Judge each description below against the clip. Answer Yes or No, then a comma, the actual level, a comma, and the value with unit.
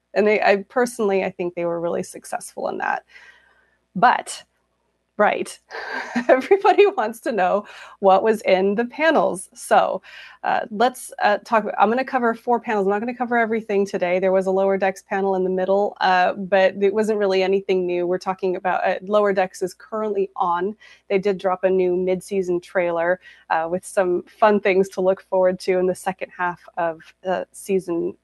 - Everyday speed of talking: Yes, average, 195 wpm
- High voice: Yes, high, 195 Hz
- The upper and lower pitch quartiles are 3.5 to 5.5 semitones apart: No, average, 2.8 semitones